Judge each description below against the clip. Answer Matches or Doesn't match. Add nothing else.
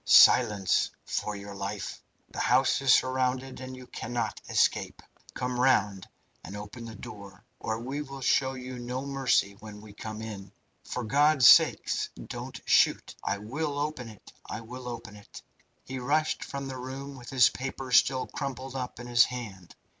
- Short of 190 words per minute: Matches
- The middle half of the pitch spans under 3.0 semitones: Doesn't match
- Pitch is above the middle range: Doesn't match